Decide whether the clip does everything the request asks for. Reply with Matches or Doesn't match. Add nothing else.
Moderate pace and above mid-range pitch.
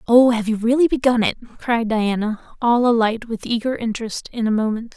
Matches